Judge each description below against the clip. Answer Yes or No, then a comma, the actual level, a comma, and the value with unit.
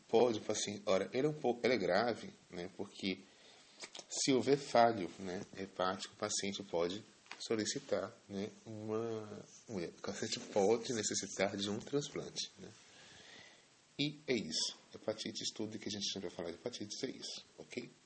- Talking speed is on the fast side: No, average, 155 wpm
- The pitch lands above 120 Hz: No, low, 105 Hz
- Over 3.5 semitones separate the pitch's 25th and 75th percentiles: No, average, 3.2 semitones